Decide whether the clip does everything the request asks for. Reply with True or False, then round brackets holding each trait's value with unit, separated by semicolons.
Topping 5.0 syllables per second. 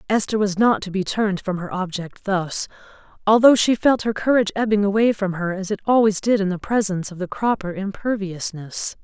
True (5.5 syllables/s)